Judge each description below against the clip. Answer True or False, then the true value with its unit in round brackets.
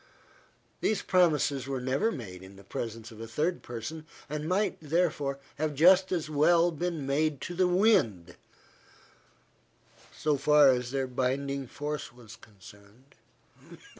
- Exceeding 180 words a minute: False (135 wpm)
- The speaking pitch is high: False (140 Hz)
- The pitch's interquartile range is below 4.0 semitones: False (5.1 semitones)